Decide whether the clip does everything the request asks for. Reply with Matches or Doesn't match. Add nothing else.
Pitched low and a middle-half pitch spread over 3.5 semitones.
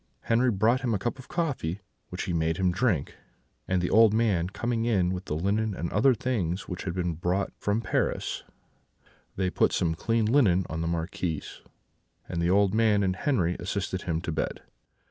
Matches